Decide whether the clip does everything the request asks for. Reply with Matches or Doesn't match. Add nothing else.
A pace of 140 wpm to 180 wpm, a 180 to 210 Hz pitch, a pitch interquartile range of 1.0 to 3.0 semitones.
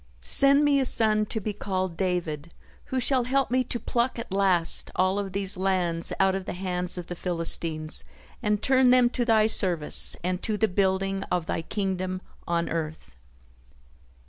Doesn't match